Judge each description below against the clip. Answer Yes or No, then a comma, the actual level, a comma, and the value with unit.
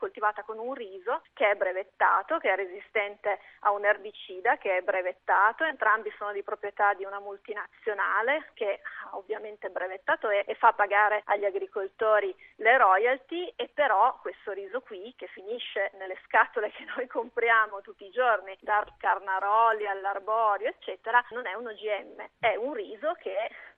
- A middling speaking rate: Yes, average, 155 wpm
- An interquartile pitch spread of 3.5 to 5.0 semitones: No, average, 3.0 semitones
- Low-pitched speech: No, high, 210 Hz